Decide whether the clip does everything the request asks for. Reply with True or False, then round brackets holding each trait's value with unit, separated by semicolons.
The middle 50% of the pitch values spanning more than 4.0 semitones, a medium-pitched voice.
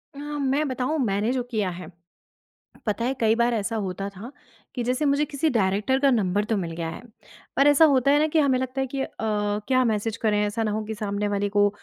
False (4.6 semitones; 225 Hz)